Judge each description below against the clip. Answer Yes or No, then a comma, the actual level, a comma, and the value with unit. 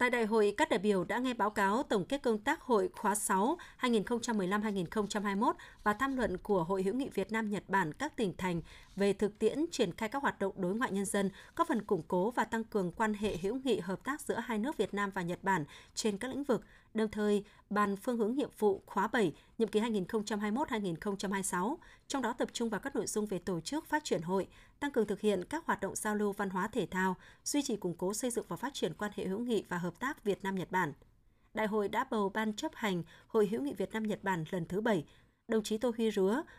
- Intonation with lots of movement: No, average, 3.3 semitones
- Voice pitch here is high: Yes, high, 210 Hz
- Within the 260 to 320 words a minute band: No, average, 245 wpm